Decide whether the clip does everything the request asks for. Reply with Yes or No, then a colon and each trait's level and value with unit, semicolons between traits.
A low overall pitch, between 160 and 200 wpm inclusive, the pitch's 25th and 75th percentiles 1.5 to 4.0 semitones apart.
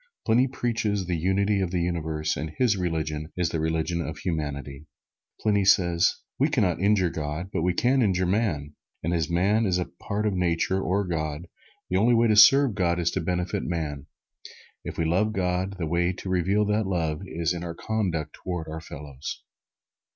Yes: very low, 90 Hz; average, 190 wpm; average, 3.7 semitones